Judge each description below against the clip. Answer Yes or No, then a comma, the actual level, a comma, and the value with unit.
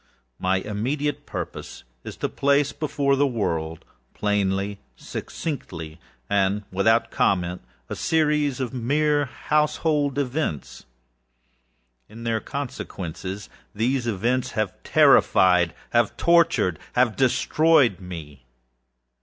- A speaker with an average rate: No, slow, 95 wpm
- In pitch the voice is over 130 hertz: No, low, 115 Hz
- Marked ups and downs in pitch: Yes, wide, 7.0 semitones